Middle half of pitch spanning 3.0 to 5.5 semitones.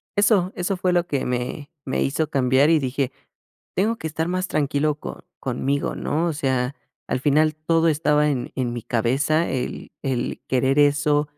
Yes: average, 3.3 semitones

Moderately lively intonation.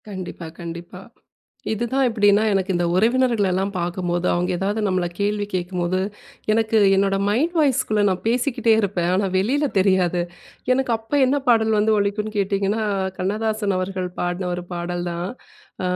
Yes: average, 3.4 semitones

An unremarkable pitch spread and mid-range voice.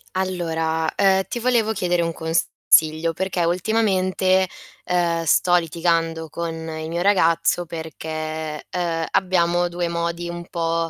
No: narrow, 1.9 semitones; medium, 170 Hz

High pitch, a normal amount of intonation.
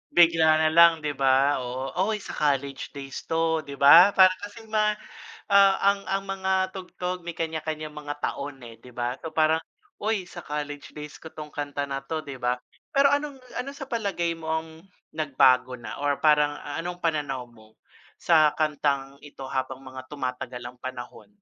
No: medium, 150 Hz; average, 4.2 semitones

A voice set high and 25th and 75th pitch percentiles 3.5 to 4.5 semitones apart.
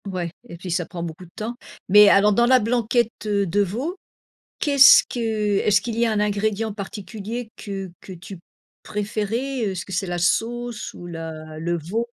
Yes: high, 205 Hz; average, 4.1 semitones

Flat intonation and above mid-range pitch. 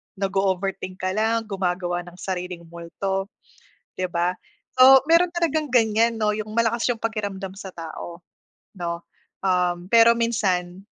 No: average, 4.1 semitones; high, 195 Hz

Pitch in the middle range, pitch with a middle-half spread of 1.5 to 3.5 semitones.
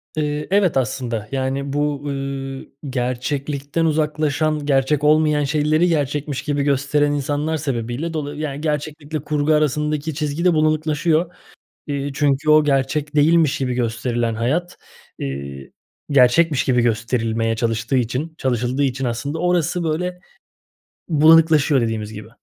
Yes: medium, 145 Hz; average, 3.0 semitones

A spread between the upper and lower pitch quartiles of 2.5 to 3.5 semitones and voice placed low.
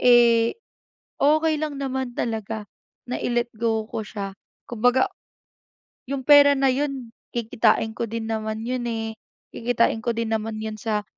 No: average, 2.9 semitones; high, 230 Hz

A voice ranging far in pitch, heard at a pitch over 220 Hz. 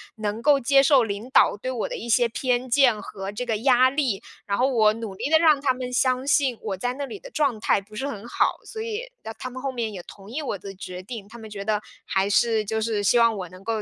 No: average, 4.1 semitones; high, 235 Hz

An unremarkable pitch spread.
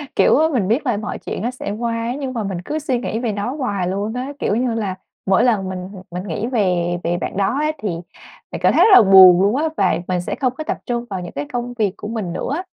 Yes: average, 4.7 semitones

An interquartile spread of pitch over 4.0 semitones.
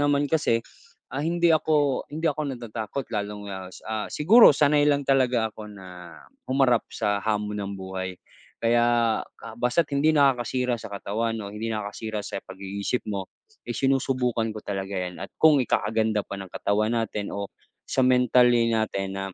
Yes: average, 4.6 semitones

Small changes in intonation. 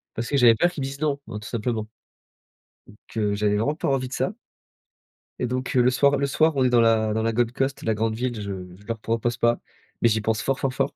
No: average, 3.4 semitones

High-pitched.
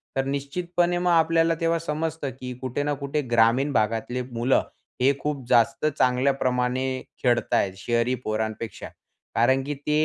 No: low, 135 Hz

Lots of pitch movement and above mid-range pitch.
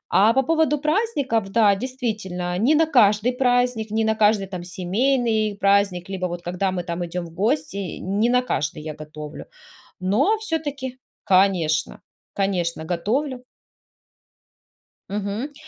Yes: wide, 5.7 semitones; high, 210 Hz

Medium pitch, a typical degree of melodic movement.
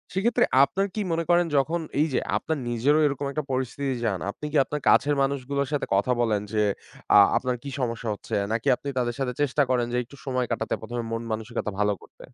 No: low, 130 Hz; average, 3.8 semitones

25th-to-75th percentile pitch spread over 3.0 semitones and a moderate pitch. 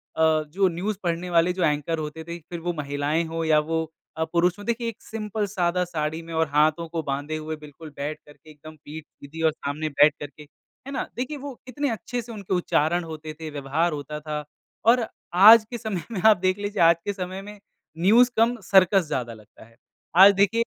Yes: average, 4.8 semitones; medium, 165 Hz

